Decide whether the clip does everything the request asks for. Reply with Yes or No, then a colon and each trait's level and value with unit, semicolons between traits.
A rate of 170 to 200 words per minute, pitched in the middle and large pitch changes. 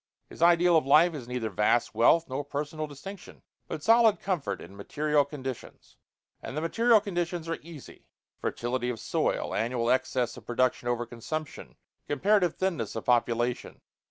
No: average, 155 wpm; medium, 145 Hz; wide, 5.9 semitones